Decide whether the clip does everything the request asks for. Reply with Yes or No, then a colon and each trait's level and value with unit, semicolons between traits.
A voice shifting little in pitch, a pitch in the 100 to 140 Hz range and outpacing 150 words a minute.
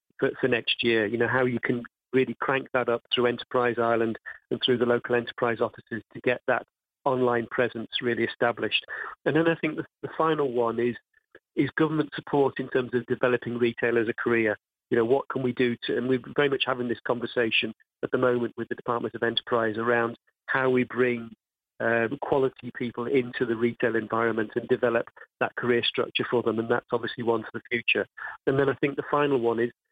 Yes: narrow, 1.8 semitones; low, 120 Hz; fast, 205 wpm